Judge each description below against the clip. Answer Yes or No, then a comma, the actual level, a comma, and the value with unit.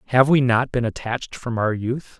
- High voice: No, low, 120 Hz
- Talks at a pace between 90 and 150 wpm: No, fast, 220 wpm